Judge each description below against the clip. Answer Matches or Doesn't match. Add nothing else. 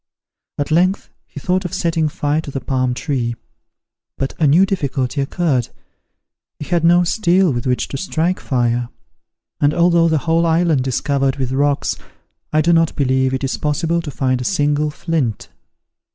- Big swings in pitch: Doesn't match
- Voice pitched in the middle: Matches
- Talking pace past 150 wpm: Matches